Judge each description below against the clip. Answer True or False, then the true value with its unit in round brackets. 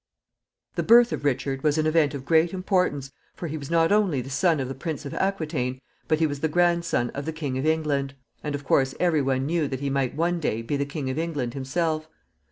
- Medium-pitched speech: True (150 Hz)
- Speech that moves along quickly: True (240 wpm)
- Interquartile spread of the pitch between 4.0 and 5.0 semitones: False (3.3 semitones)